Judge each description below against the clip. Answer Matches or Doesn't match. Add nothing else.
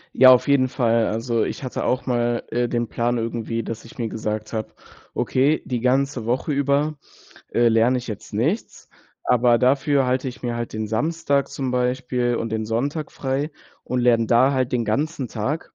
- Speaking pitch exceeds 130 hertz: Doesn't match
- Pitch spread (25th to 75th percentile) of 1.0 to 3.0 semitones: Matches